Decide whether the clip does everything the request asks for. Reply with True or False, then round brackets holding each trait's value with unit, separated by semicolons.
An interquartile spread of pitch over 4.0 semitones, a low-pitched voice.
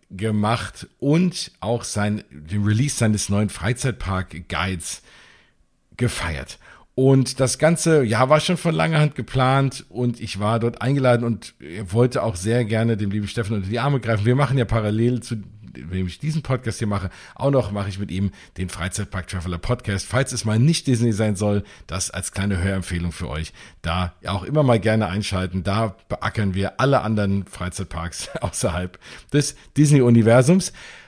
True (4.7 semitones; 110 Hz)